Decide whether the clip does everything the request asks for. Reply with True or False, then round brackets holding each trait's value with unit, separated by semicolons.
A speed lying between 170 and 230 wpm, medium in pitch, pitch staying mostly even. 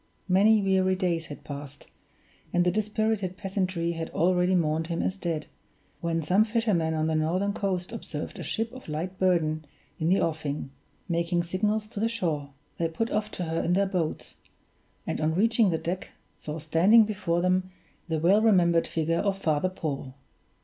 False (175 wpm; 180 Hz; 3.5 semitones)